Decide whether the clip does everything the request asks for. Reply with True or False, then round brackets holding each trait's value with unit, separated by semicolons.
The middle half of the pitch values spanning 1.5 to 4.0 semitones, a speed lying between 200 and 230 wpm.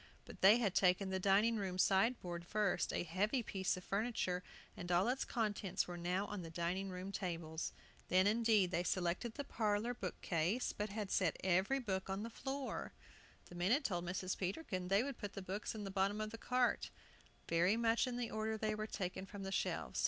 True (3.3 semitones; 205 wpm)